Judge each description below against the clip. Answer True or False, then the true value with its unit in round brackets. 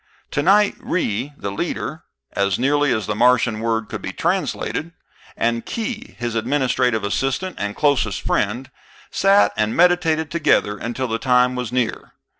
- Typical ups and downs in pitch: True (4.9 semitones)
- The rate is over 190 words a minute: False (145 wpm)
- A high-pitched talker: False (125 Hz)